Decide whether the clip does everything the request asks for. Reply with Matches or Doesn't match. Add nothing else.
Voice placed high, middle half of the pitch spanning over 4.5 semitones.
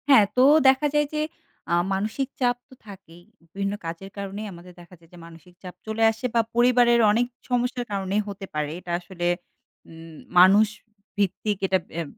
Matches